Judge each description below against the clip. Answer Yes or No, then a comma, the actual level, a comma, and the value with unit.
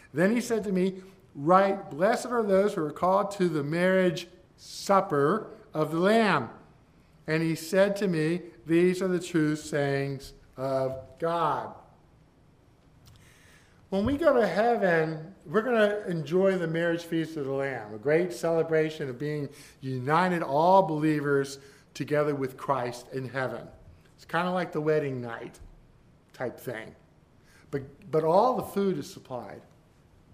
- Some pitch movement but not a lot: Yes, average, 4.7 semitones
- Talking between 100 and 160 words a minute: Yes, average, 150 wpm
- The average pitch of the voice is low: No, medium, 165 Hz